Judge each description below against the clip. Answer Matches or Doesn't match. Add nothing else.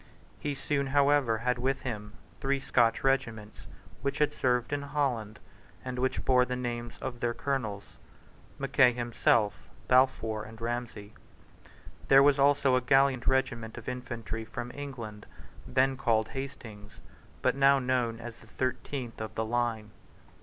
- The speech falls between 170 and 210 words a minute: Doesn't match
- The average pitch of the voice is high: Doesn't match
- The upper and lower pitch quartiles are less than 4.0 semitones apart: Matches